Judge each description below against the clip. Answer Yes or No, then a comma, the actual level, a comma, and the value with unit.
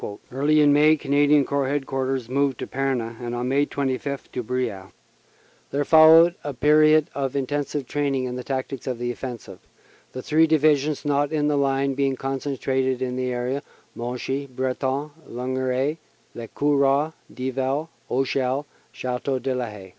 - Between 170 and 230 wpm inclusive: No, average, 155 wpm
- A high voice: No, low, 135 Hz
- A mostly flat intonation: Yes, narrow, 2.2 semitones